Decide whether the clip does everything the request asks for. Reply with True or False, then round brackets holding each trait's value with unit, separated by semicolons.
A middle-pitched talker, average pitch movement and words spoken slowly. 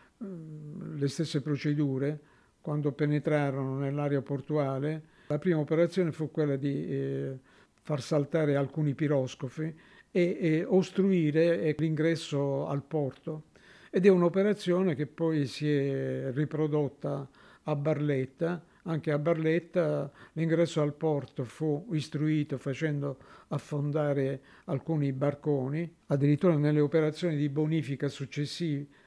False (150 Hz; 2.2 semitones; 105 wpm)